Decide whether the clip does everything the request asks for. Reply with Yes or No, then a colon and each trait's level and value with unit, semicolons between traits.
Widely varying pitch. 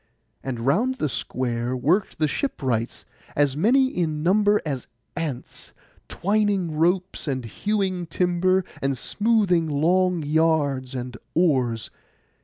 Yes: wide, 5.8 semitones